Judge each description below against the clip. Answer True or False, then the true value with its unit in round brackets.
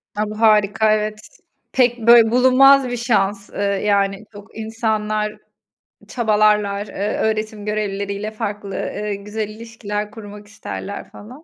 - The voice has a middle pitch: False (215 Hz)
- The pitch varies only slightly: True (1.3 semitones)